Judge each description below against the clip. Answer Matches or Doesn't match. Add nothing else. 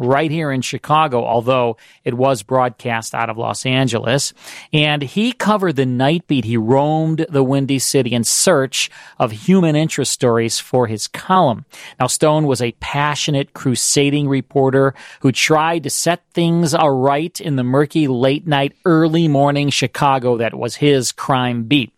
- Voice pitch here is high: Doesn't match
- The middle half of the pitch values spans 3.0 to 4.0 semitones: Matches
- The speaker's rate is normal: Matches